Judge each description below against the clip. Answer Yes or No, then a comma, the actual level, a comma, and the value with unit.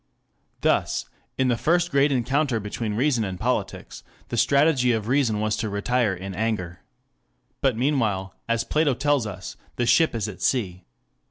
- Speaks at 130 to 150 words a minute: No, average, 160 wpm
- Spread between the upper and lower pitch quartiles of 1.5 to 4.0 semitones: No, average, 4.9 semitones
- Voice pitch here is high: No, low, 115 Hz